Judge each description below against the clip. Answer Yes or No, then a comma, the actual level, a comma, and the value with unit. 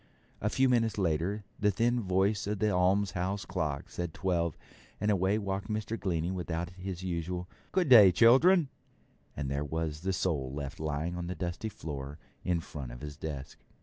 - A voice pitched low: Yes, very low, 90 Hz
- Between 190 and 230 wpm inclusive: No, average, 175 wpm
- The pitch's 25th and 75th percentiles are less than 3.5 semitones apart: No, average, 4.3 semitones